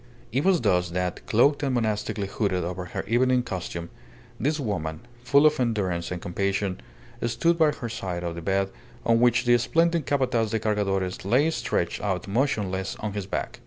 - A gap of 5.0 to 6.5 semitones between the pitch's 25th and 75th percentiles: Yes, wide, 5.4 semitones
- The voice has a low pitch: Yes, low, 105 Hz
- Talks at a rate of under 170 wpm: No, average, 175 wpm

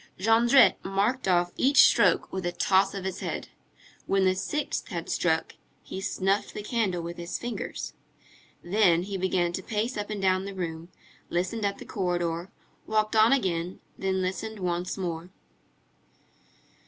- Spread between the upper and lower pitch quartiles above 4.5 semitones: No, average, 3.1 semitones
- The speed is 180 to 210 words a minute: No, average, 155 wpm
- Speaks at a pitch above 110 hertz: Yes, high, 190 Hz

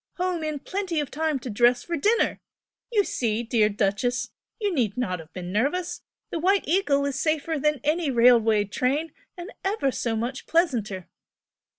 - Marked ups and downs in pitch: Yes, wide, 6.3 semitones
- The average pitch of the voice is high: Yes, very high, 275 Hz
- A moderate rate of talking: Yes, average, 170 wpm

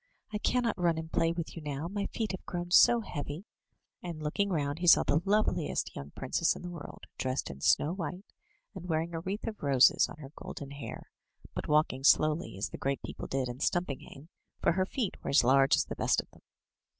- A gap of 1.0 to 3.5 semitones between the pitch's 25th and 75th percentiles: No, average, 4.3 semitones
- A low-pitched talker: No, medium, 160 Hz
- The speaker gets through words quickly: Yes, fast, 215 wpm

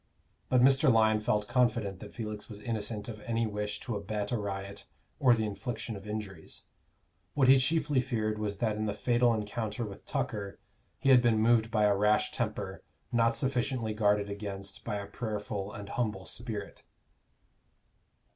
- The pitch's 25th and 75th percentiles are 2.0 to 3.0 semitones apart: Yes, narrow, 2.6 semitones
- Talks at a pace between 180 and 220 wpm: No, average, 165 wpm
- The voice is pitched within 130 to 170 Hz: No, low, 110 Hz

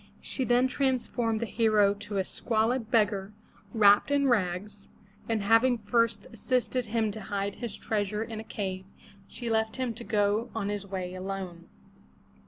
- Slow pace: No, average, 160 wpm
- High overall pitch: Yes, high, 215 Hz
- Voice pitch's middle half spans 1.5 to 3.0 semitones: Yes, narrow, 2.6 semitones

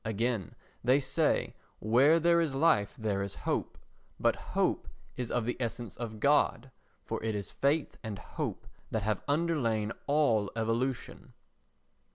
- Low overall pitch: Yes, low, 120 Hz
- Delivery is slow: No, average, 145 wpm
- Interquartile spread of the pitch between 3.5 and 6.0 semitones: Yes, average, 4.6 semitones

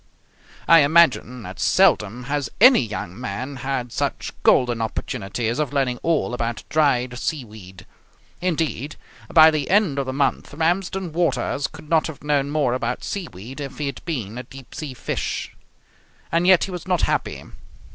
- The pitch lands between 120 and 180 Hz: Yes, medium, 140 Hz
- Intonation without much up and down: No, average, 4.8 semitones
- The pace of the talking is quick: No, average, 160 wpm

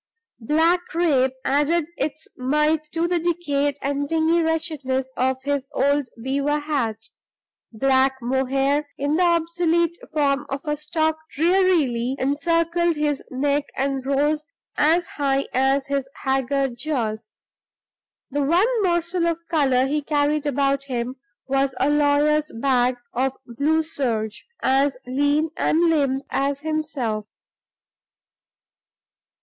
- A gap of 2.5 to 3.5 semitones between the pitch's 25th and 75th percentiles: Yes, average, 3.0 semitones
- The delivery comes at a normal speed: No, slow, 120 wpm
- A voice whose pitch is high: Yes, very high, 285 Hz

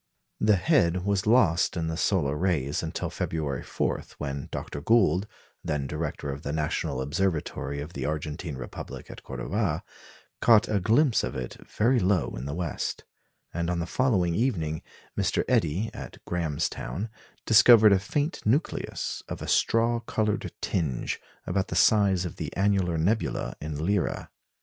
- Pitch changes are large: Yes, wide, 5.7 semitones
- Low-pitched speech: Yes, very low, 90 Hz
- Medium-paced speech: Yes, average, 155 wpm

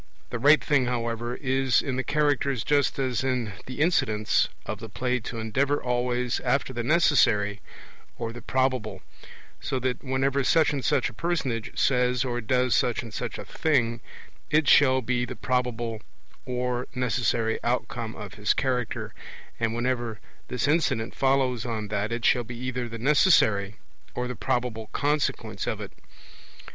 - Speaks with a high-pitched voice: No, low, 125 Hz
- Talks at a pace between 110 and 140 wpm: No, average, 160 wpm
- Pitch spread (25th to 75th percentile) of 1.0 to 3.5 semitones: Yes, narrow, 2.4 semitones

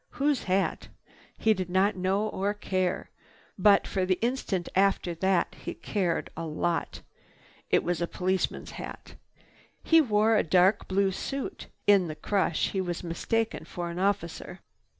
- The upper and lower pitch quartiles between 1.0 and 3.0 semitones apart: Yes, average, 2.7 semitones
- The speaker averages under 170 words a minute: Yes, average, 150 wpm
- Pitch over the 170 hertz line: Yes, high, 190 Hz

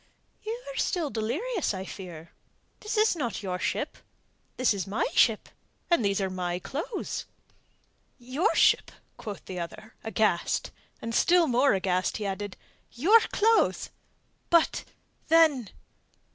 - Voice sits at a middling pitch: No, high, 230 Hz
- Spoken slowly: Yes, slow, 130 wpm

